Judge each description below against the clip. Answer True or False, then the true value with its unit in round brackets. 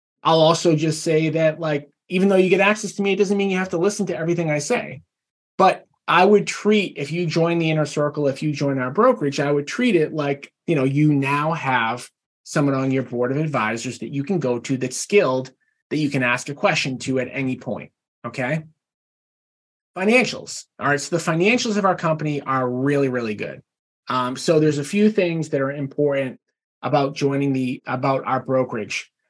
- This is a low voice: False (150 Hz)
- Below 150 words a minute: False (205 wpm)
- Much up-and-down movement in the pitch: False (4.3 semitones)